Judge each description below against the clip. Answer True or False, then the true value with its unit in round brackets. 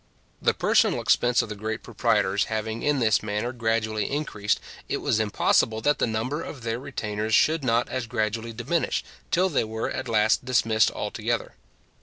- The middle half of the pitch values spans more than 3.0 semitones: False (2.5 semitones)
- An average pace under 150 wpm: False (170 wpm)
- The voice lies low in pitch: True (115 Hz)